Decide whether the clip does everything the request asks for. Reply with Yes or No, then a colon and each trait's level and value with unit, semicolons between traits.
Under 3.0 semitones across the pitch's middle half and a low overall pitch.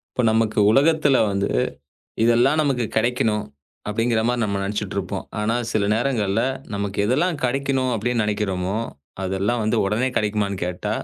No: average, 3.5 semitones; low, 110 Hz